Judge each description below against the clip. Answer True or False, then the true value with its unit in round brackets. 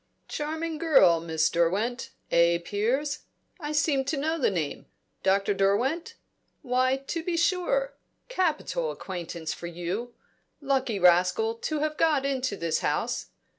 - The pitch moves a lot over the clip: True (8.9 semitones)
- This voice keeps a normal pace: False (130 wpm)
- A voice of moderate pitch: False (255 Hz)